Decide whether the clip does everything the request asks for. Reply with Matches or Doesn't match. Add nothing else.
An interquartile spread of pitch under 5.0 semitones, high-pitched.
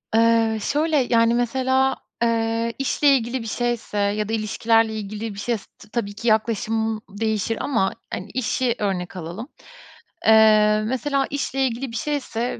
Matches